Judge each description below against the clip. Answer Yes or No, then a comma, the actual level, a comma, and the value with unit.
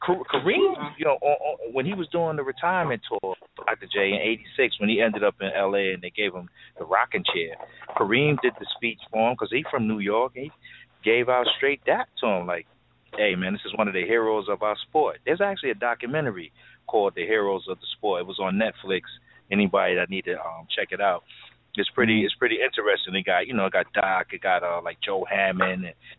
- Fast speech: Yes, fast, 230 wpm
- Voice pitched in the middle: No, low, 120 Hz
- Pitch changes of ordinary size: No, wide, 7.0 semitones